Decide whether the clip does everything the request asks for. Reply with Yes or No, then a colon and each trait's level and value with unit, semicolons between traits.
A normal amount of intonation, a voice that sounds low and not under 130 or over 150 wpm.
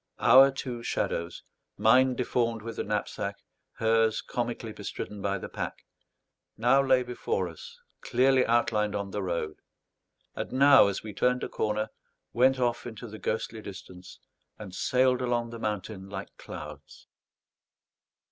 Yes: average, 3.5 semitones; low, 115 Hz; average, 140 wpm